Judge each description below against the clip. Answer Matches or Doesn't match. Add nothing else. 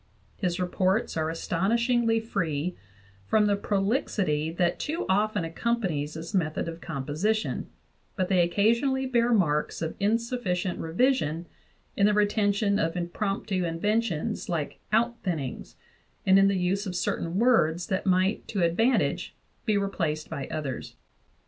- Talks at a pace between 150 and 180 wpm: Doesn't match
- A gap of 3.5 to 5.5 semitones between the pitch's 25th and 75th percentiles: Matches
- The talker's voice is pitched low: Doesn't match